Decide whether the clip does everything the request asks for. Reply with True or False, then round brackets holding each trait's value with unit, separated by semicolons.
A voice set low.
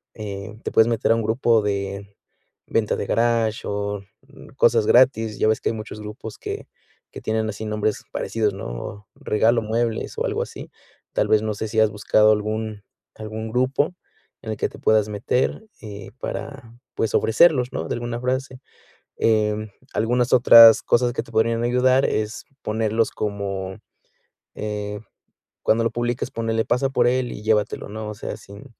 True (110 Hz)